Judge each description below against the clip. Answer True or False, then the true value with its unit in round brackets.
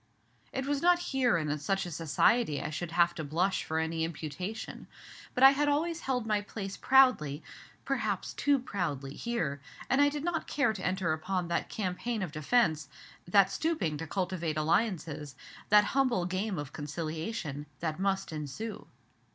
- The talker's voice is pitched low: False (185 Hz)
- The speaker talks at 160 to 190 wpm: True (170 wpm)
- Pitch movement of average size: False (7.2 semitones)